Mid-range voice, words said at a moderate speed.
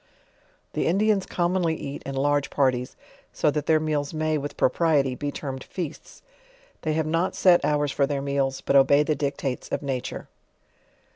Yes: medium, 145 Hz; average, 170 wpm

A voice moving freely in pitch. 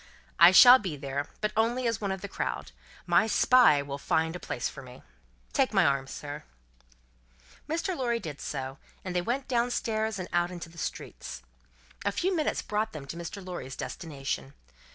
Yes: wide, 7.8 semitones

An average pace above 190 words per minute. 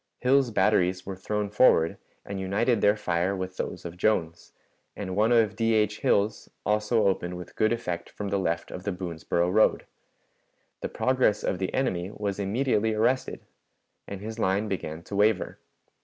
No: average, 170 wpm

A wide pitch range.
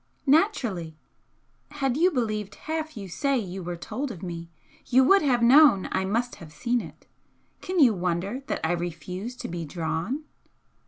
Yes: wide, 7.6 semitones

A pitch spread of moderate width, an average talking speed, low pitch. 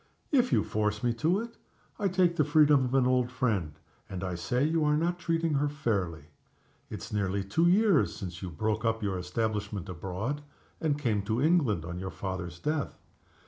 No: wide, 7.9 semitones; average, 185 wpm; low, 115 Hz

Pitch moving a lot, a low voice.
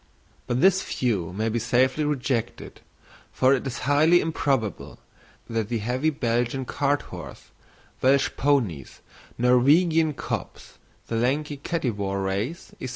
No: average, 4.2 semitones; low, 130 Hz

